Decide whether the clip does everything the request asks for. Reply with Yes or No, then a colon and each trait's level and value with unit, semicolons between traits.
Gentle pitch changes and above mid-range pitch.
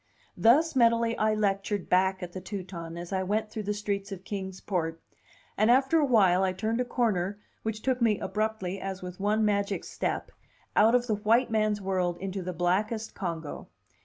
No: average, 3.0 semitones; high, 205 Hz